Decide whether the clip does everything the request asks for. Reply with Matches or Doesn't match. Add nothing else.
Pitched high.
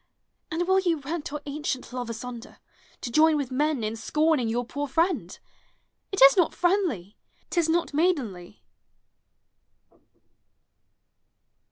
Matches